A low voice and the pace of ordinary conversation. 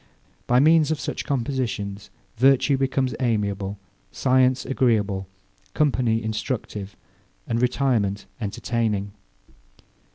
No: low, 120 Hz; slow, 90 wpm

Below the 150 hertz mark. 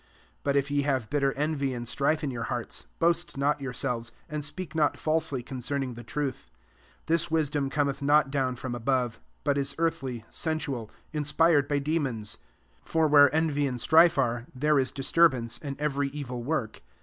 Yes: medium, 140 Hz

